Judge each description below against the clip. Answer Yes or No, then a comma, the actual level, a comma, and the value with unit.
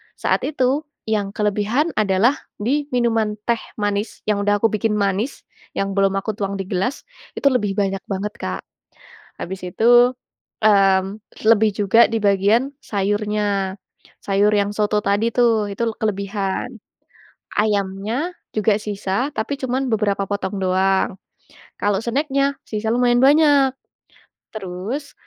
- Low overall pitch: No, high, 210 Hz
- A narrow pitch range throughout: No, average, 3.2 semitones